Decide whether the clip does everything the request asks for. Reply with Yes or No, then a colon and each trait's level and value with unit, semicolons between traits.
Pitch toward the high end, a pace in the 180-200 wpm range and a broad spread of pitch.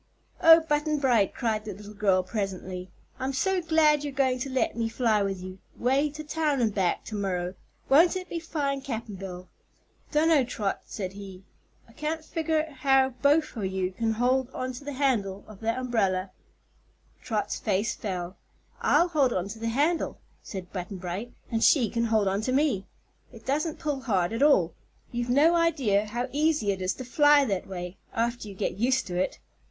Yes: high, 235 Hz; average, 190 wpm; wide, 6.5 semitones